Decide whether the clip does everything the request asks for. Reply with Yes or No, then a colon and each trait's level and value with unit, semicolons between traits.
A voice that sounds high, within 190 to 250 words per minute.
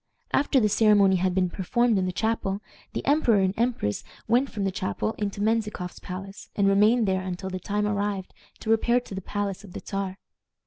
Yes: high, 200 Hz; average, 195 wpm